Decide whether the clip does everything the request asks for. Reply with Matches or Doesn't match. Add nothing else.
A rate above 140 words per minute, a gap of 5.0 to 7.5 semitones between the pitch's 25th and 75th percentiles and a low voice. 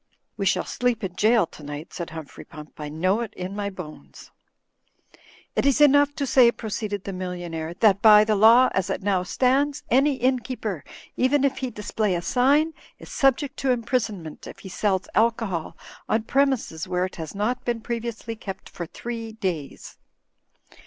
Doesn't match